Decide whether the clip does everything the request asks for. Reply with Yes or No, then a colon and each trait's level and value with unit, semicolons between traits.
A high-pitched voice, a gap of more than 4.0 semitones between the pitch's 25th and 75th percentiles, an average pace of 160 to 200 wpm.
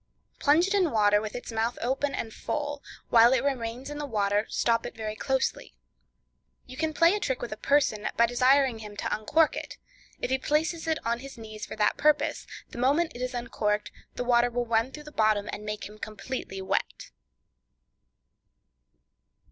Yes: high, 245 Hz; average, 4.8 semitones; average, 190 wpm